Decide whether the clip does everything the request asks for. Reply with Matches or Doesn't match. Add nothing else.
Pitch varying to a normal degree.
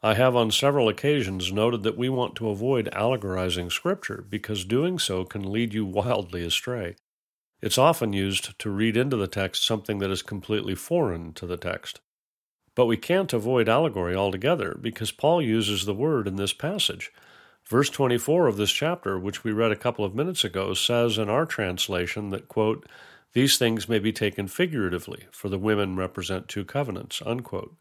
Matches